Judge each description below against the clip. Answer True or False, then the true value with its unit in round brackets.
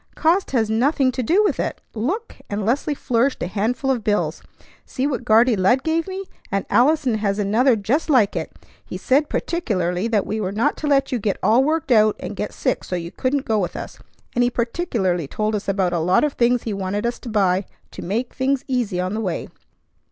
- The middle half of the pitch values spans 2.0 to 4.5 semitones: False (5.0 semitones)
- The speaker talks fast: True (220 wpm)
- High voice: True (230 Hz)